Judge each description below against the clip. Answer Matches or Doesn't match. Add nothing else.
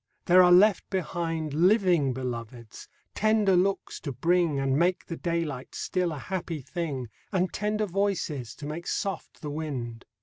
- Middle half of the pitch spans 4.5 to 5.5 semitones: Matches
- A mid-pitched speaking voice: Matches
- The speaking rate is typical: Matches